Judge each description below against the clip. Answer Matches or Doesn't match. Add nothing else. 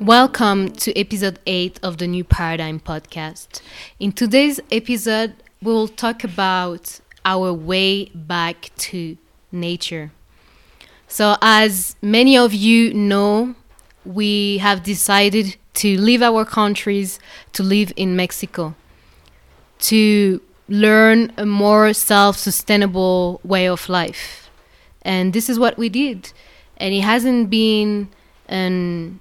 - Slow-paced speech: Matches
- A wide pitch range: Doesn't match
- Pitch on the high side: Matches